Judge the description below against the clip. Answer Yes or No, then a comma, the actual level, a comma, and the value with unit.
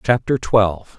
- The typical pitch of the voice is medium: No, low, 110 Hz